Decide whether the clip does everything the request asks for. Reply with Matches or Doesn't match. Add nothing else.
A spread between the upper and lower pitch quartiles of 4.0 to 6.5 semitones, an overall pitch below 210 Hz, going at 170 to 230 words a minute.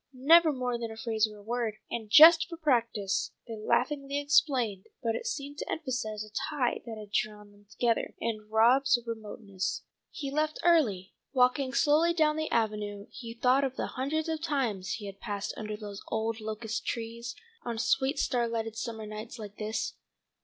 Doesn't match